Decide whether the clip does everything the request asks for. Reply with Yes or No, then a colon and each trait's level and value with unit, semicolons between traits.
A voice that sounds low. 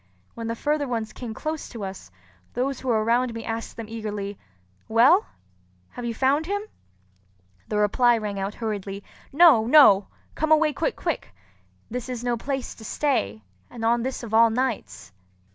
No: high, 235 Hz